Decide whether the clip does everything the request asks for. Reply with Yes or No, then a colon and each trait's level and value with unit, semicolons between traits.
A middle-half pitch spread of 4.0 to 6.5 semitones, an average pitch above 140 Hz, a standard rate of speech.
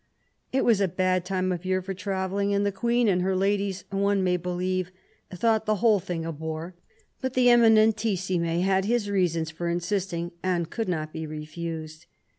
No: average, 2.9 semitones; medium, 185 Hz; average, 180 wpm